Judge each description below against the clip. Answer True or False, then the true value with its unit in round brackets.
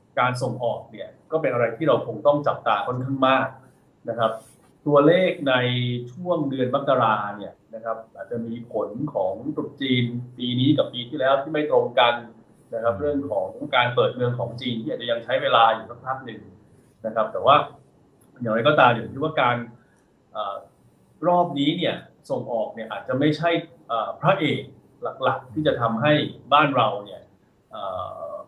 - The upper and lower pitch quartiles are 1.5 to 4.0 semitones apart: True (3.5 semitones)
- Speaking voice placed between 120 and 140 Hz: True (125 Hz)